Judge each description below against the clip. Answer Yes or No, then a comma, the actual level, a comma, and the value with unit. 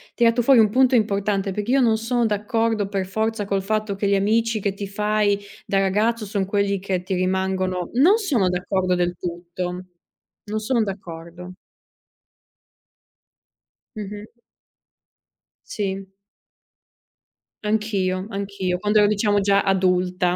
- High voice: Yes, high, 200 Hz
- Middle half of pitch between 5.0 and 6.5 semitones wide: No, narrow, 2.5 semitones